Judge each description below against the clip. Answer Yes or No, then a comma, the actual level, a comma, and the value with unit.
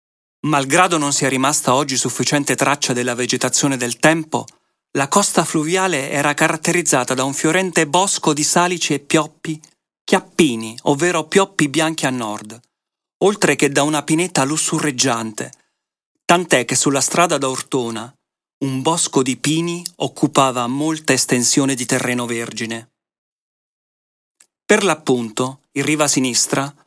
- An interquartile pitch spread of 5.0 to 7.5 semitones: No, average, 3.8 semitones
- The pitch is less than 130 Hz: No, medium, 140 Hz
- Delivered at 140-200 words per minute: No, average, 125 wpm